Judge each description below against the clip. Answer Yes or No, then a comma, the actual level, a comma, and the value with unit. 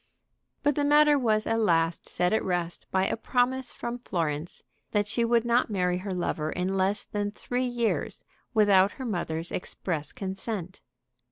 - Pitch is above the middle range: Yes, high, 205 Hz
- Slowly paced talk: No, average, 165 wpm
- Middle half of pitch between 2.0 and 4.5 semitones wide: No, average, 4.9 semitones